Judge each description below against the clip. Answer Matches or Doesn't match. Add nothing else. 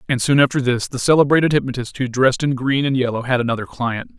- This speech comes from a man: Matches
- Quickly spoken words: Matches